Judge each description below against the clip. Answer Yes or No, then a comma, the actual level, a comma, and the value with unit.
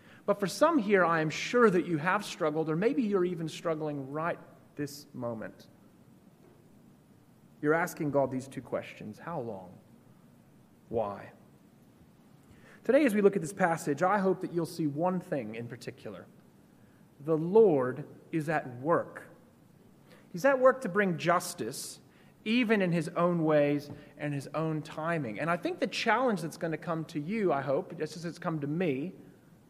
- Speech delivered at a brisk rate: No, average, 170 wpm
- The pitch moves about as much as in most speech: Yes, average, 4.0 semitones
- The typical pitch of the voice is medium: Yes, medium, 165 Hz